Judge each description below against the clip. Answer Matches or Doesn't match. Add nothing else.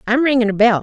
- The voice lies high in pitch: Matches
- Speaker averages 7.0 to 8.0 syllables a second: Matches